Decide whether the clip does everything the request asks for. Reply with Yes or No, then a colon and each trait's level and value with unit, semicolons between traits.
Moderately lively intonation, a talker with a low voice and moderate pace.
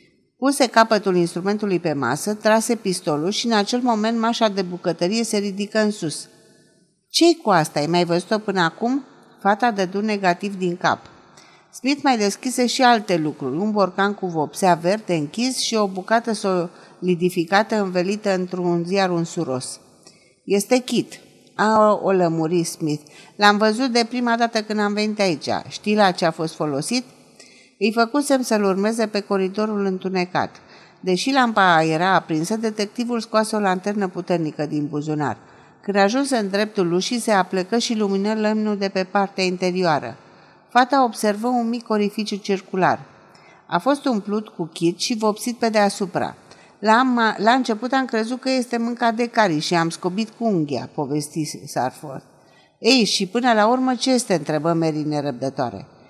No: average, 4.4 semitones; high, 200 Hz; average, 155 wpm